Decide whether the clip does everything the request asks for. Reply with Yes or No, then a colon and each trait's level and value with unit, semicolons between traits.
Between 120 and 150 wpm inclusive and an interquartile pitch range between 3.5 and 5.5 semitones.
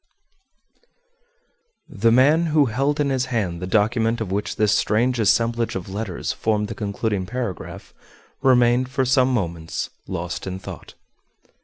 Yes: average, 145 wpm; average, 4.2 semitones